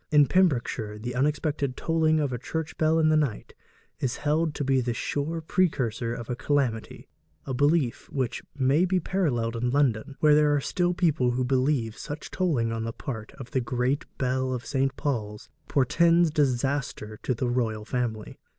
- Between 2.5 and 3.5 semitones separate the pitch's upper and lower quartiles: No, average, 4.0 semitones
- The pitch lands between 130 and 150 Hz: Yes, low, 135 Hz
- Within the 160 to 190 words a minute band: Yes, average, 180 wpm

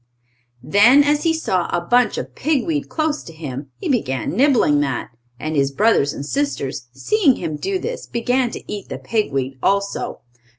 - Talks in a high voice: Yes, high, 210 Hz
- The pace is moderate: Yes, average, 180 wpm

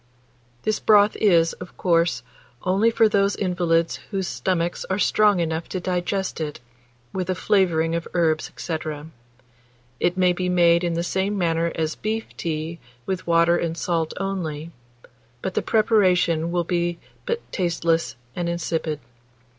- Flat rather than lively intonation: Yes, narrow, 2.3 semitones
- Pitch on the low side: No, medium, 175 Hz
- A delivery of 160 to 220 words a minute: No, average, 145 wpm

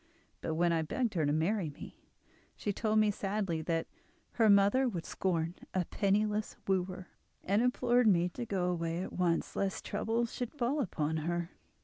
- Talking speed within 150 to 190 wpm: Yes, average, 170 wpm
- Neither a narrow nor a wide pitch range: Yes, average, 4.3 semitones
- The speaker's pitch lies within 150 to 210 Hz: Yes, high, 190 Hz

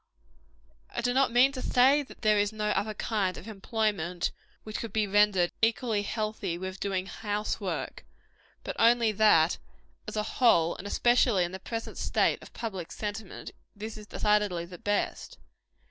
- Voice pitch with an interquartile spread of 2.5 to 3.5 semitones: Yes, average, 2.9 semitones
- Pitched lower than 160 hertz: No, high, 210 Hz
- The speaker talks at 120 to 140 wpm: No, average, 165 wpm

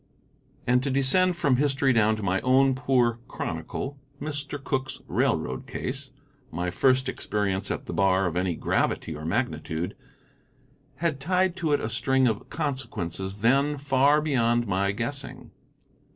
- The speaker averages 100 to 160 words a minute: Yes, average, 145 wpm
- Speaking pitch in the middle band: No, low, 130 Hz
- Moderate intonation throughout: No, wide, 6.1 semitones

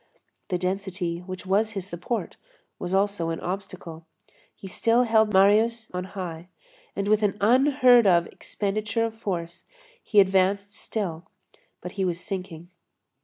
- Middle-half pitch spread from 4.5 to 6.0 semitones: No, average, 3.0 semitones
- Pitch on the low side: No, high, 195 Hz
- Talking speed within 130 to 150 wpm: Yes, average, 140 wpm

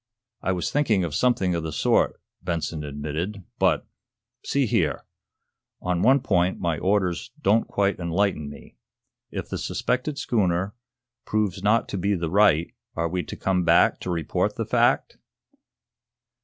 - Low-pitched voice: Yes, very low, 90 Hz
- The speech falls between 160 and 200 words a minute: No, average, 150 wpm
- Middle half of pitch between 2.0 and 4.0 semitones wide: Yes, average, 3.6 semitones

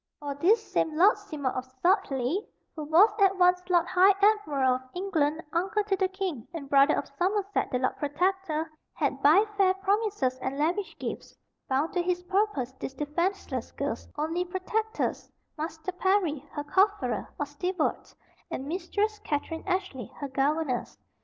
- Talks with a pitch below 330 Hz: No, very high, 340 Hz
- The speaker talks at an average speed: Yes, average, 155 wpm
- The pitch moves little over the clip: No, average, 5.1 semitones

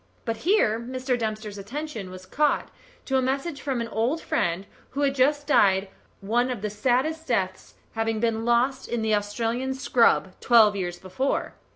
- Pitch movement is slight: No, average, 4.1 semitones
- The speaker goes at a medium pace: Yes, average, 175 wpm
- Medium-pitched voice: No, high, 235 Hz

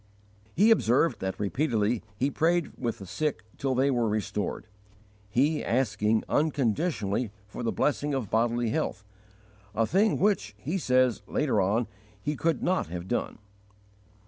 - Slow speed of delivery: No, average, 145 wpm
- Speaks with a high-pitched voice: No, low, 125 Hz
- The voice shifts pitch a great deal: Yes, wide, 6.0 semitones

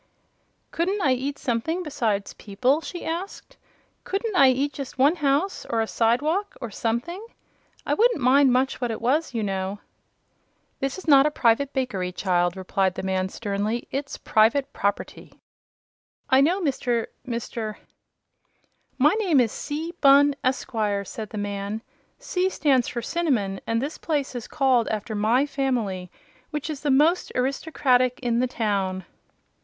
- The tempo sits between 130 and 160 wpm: Yes, average, 155 wpm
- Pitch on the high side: Yes, very high, 255 Hz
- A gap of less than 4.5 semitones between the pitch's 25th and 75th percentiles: No, average, 5.1 semitones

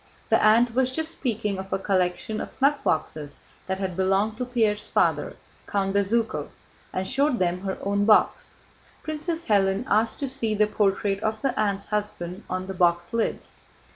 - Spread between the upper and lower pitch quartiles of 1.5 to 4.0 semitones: Yes, average, 3.4 semitones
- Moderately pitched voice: No, high, 210 Hz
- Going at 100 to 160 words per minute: No, average, 170 wpm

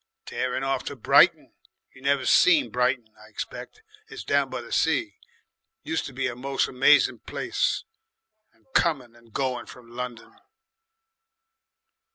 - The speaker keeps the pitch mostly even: Yes, narrow, 2.2 semitones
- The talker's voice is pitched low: Yes, low, 130 Hz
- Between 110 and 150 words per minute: Yes, average, 140 wpm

